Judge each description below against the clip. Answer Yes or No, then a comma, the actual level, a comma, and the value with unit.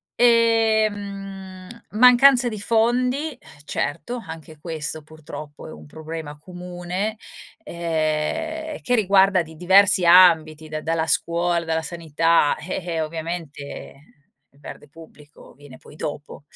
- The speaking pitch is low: No, medium, 170 Hz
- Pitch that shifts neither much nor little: Yes, average, 4.6 semitones